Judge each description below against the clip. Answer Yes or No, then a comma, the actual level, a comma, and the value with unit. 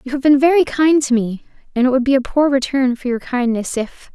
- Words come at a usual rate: No, fast, 260 wpm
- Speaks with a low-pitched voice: No, very high, 265 Hz